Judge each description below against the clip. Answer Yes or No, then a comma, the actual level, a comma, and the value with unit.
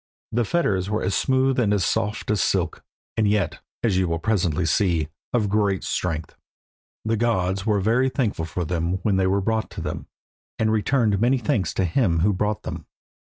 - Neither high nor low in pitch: No, low, 105 Hz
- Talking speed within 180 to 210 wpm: Yes, average, 190 wpm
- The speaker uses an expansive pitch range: No, average, 3.5 semitones